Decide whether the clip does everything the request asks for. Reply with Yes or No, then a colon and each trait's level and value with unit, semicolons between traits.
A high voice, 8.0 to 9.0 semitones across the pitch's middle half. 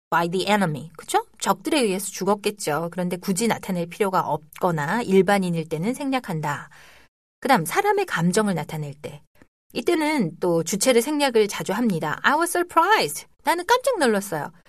Yes: high, 200 Hz; wide, 8.4 semitones